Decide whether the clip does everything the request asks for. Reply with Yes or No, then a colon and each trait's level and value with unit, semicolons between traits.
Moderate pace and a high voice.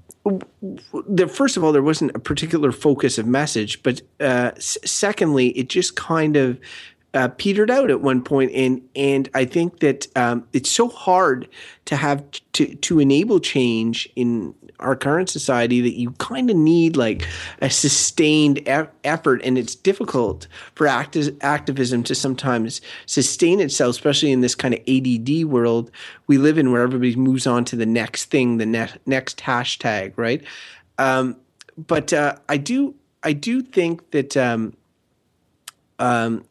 No: average, 160 wpm; low, 135 Hz